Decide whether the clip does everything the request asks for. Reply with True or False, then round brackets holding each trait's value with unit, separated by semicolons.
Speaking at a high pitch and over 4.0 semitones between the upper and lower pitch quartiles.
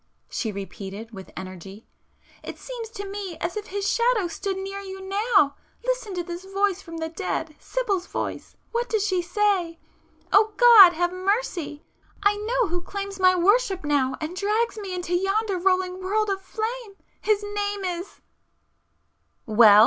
False (385 Hz; 3.3 semitones)